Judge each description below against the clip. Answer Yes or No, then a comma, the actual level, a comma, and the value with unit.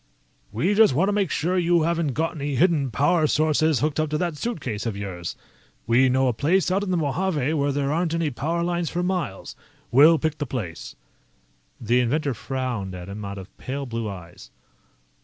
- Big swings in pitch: Yes, wide, 5.7 semitones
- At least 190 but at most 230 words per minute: Yes, average, 195 wpm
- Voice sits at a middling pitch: Yes, medium, 145 Hz